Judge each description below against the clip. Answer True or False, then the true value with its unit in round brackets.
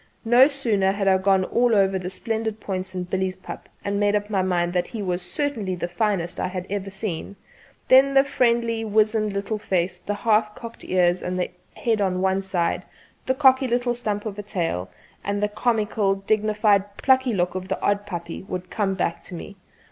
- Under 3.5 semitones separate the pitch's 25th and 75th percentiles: True (3.0 semitones)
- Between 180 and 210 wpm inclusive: True (200 wpm)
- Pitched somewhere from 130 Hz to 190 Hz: False (200 Hz)